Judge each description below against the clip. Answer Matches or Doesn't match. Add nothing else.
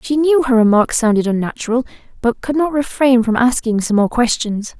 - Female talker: Matches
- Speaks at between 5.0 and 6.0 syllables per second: Matches